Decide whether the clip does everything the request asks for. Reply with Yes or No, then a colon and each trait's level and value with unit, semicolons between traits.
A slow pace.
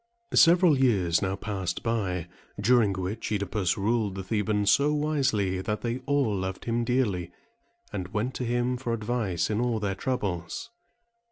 No: average, 155 wpm